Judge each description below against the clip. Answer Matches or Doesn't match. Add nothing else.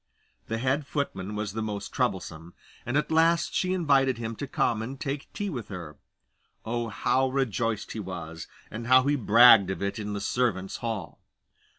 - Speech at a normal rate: Matches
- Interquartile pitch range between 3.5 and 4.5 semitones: Doesn't match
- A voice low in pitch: Matches